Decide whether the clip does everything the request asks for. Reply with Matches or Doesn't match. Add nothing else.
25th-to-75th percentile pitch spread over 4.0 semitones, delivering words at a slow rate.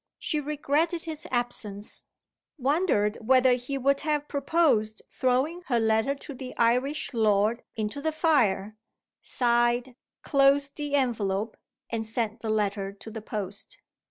Matches